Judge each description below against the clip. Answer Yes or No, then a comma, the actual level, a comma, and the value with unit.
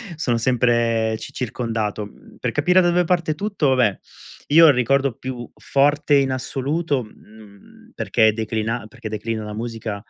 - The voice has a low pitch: Yes, low, 120 Hz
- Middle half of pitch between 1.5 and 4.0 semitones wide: No, average, 4.5 semitones